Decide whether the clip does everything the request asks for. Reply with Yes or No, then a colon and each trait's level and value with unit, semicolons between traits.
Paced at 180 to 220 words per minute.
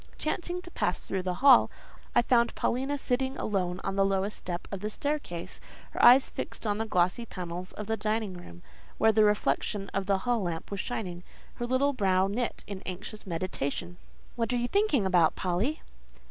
Yes: average, 190 wpm